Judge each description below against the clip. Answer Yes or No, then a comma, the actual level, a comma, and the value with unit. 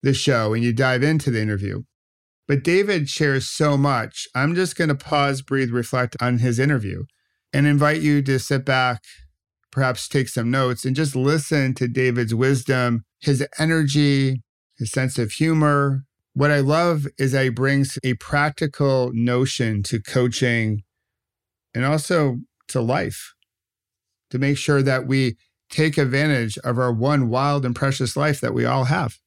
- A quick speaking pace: No, average, 160 wpm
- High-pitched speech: No, low, 130 Hz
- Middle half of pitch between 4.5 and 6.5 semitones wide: No, average, 3.1 semitones